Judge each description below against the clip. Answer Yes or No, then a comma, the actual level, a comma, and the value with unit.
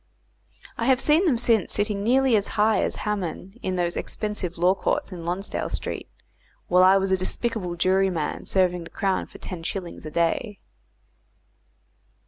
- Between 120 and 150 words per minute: No, average, 165 wpm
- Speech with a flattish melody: No, average, 3.2 semitones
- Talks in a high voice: Yes, high, 195 Hz